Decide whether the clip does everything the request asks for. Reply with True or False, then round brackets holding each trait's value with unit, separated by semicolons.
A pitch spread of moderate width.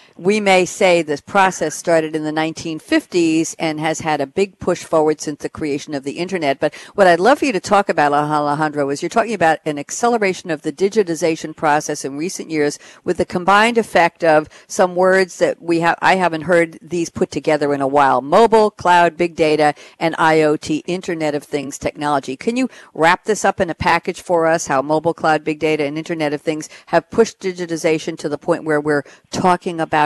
True (3.2 semitones)